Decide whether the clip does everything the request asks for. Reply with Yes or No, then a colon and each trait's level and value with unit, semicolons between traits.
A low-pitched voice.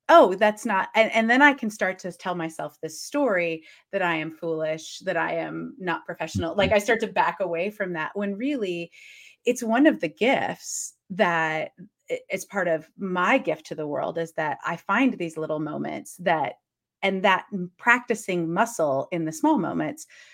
No: high, 190 Hz